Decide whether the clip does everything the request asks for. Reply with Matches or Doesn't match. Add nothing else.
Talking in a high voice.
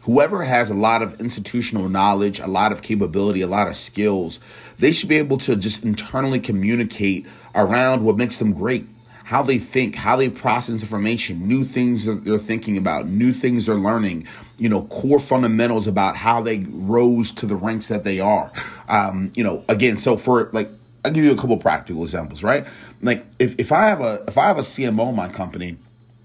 Doesn't match